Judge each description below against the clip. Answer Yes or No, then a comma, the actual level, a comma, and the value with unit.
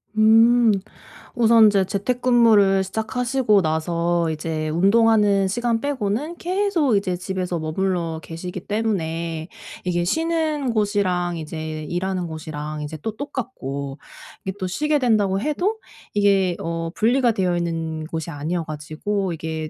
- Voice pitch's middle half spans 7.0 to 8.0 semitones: No, wide, 5.6 semitones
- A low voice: No, high, 190 Hz